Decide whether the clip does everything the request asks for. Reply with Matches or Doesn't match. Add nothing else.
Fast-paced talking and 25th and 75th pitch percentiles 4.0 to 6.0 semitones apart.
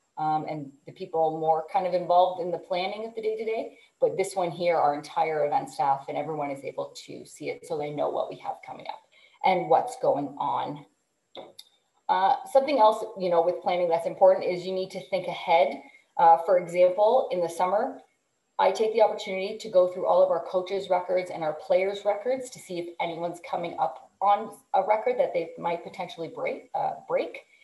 Matches